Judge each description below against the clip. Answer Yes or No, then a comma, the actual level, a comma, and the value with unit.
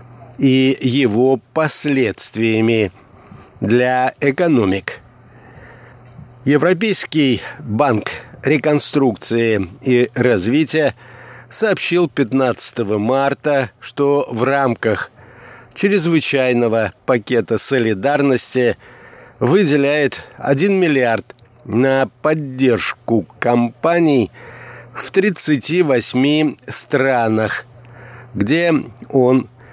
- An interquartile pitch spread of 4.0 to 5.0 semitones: No, average, 3.3 semitones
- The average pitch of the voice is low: Yes, low, 130 Hz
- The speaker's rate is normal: No, slow, 60 wpm